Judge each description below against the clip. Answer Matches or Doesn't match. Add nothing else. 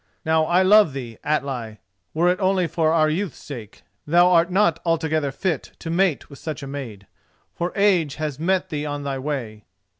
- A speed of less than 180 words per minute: Doesn't match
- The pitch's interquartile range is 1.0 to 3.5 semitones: Doesn't match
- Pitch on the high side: Doesn't match